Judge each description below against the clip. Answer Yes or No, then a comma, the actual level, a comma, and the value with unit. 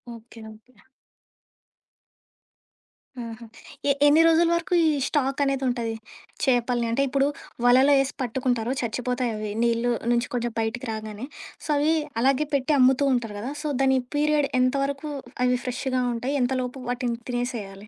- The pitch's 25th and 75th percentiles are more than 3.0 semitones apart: No, narrow, 2.5 semitones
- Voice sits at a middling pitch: No, very high, 250 Hz